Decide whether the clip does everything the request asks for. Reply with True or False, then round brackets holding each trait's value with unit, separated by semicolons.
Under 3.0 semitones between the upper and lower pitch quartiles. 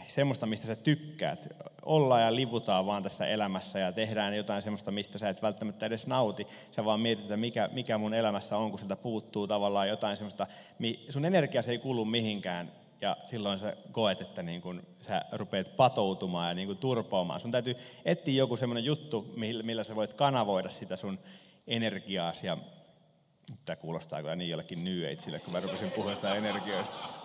False (3.5 semitones)